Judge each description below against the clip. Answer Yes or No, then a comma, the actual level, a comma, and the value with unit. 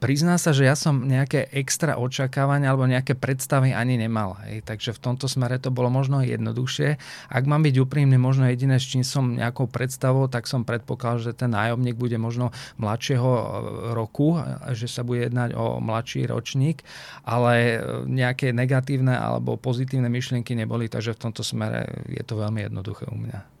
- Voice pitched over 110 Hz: Yes, low, 125 Hz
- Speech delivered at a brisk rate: Yes, fast, 170 wpm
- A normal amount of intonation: No, narrow, 2.3 semitones